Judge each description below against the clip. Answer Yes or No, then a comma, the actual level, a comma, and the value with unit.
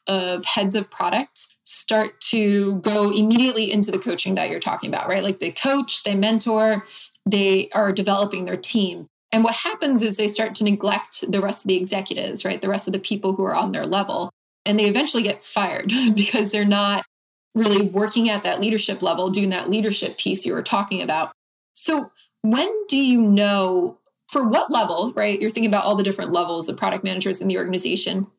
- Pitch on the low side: No, high, 205 Hz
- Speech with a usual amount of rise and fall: No, narrow, 2.0 semitones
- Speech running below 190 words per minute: No, average, 200 wpm